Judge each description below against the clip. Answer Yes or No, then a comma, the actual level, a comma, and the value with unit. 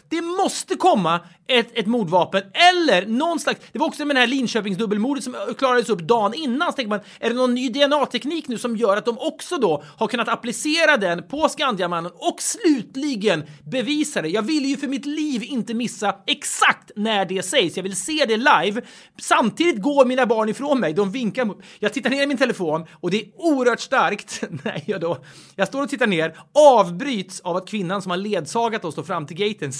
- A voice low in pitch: No, high, 235 Hz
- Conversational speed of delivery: No, fast, 205 wpm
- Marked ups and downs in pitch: Yes, wide, 5.8 semitones